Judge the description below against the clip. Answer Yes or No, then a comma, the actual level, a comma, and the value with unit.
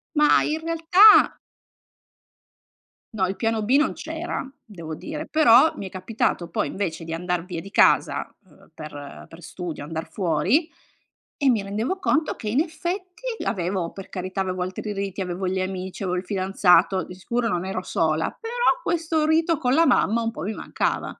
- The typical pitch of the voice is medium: No, high, 200 Hz